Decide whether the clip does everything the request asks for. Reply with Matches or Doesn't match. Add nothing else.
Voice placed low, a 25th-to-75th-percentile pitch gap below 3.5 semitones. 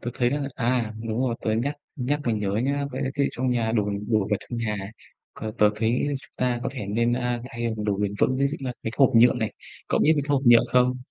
Matches